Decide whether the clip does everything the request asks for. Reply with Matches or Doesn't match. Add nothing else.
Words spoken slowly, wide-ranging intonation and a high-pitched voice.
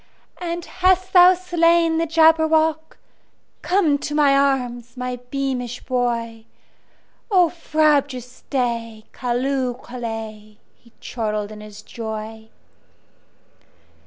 Matches